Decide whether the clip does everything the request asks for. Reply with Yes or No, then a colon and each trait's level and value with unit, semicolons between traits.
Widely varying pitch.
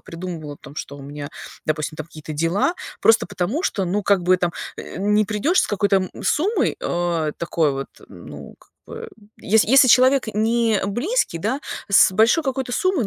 Yes: wide, 6.4 semitones